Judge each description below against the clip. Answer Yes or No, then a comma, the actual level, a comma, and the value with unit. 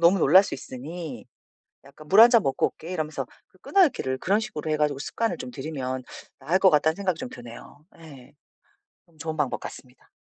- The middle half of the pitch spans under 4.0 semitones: No, average, 5.3 semitones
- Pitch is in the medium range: Yes, medium, 155 Hz